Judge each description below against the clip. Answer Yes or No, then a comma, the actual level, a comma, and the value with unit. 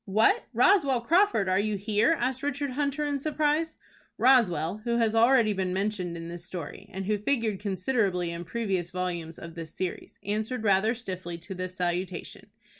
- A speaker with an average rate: Yes, average, 170 wpm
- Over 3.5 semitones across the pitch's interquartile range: Yes, wide, 5.6 semitones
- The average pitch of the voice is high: Yes, high, 205 Hz